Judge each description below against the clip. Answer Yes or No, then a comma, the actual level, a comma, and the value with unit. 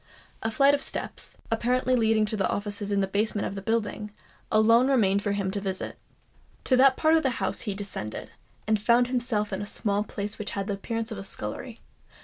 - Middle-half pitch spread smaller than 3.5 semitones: Yes, average, 2.9 semitones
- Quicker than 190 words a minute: Yes, fast, 205 wpm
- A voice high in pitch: Yes, high, 215 Hz